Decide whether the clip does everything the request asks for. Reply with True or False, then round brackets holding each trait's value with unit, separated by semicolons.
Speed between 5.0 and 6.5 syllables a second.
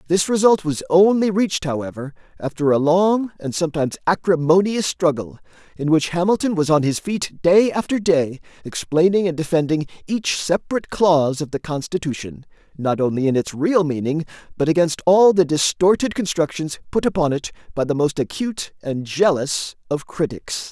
True (5.2 syllables/s)